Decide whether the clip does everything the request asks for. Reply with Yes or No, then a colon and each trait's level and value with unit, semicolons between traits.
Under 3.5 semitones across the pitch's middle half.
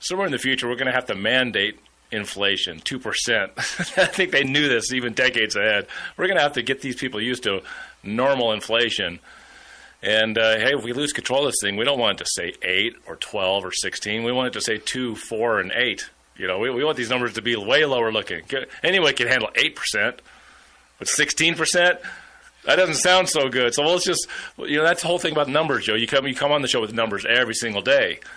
No: average, 4.8 semitones